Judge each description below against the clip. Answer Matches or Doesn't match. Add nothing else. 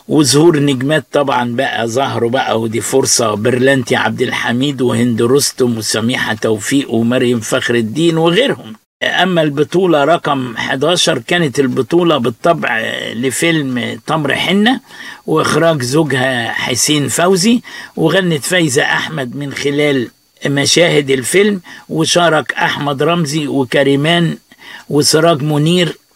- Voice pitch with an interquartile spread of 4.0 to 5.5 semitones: Matches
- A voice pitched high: Doesn't match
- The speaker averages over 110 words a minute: Doesn't match